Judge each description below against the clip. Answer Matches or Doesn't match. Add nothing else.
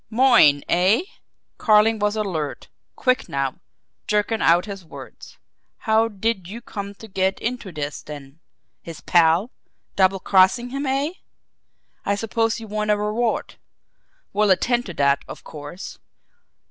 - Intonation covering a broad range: Doesn't match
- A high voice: Matches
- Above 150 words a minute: Doesn't match